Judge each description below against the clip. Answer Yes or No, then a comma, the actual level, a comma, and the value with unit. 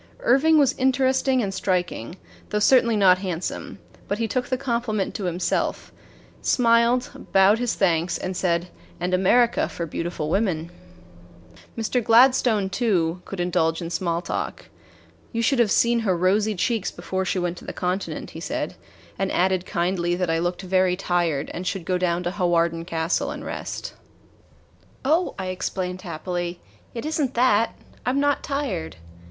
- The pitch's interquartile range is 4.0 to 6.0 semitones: Yes, average, 4.9 semitones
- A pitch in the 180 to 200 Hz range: Yes, high, 190 Hz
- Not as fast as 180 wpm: Yes, average, 160 wpm